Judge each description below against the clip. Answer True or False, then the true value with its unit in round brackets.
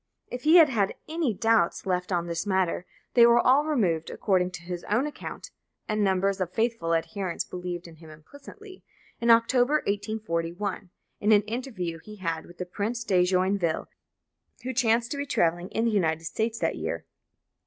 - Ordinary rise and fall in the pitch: True (4.9 semitones)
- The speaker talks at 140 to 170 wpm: False (180 wpm)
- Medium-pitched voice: False (200 Hz)